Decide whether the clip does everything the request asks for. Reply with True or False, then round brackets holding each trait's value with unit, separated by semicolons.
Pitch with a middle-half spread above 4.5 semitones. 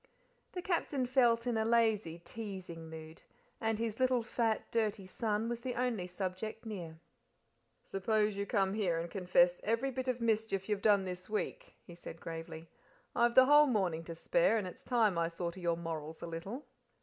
True (5.0 semitones)